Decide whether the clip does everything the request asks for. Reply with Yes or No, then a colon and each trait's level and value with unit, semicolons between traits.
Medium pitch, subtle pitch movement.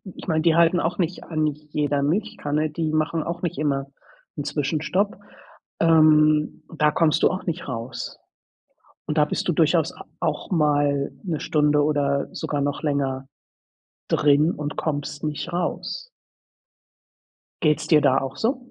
Yes: medium, 150 Hz; narrow, 2.3 semitones